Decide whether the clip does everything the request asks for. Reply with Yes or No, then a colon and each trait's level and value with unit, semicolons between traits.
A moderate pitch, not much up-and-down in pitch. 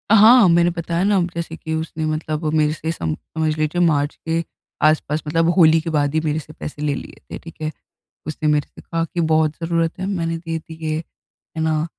Yes: medium, 160 Hz; narrow, 1.3 semitones